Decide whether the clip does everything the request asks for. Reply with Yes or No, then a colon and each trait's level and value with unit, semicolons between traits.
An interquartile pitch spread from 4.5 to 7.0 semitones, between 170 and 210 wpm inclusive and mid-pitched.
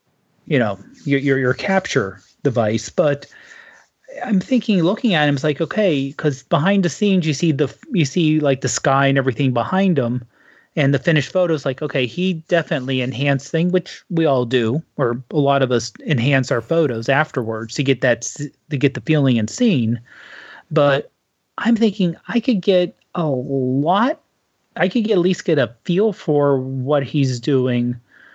Yes: average, 5.2 semitones; average, 180 wpm; medium, 150 Hz